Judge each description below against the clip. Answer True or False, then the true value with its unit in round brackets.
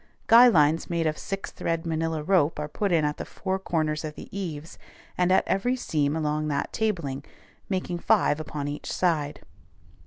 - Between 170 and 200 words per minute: True (180 wpm)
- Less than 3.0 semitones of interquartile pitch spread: False (3.7 semitones)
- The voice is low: False (160 Hz)